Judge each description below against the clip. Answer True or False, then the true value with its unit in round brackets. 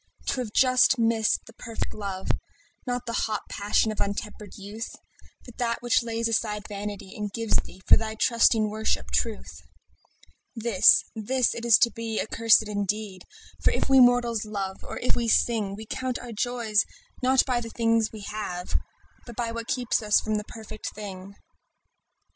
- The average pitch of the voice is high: True (220 Hz)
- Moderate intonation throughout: False (2.1 semitones)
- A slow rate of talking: False (175 wpm)